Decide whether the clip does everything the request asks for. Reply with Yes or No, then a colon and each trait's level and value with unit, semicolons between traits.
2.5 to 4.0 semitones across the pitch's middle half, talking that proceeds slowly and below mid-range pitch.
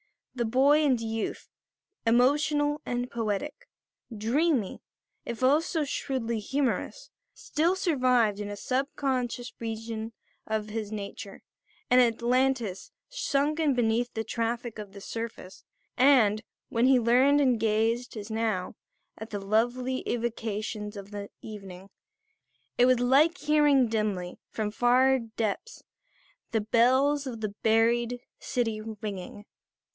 No: average, 3.3 semitones; slow, 120 wpm; high, 235 Hz